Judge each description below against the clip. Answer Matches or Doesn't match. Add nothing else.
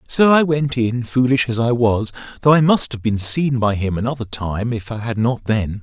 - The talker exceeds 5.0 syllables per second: Doesn't match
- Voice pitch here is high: Doesn't match